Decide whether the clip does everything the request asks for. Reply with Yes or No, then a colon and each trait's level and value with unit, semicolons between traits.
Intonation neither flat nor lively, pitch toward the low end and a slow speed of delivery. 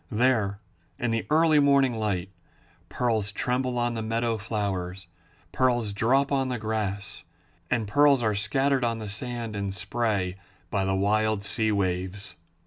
No: average, 3.5 semitones; low, 110 Hz; average, 145 wpm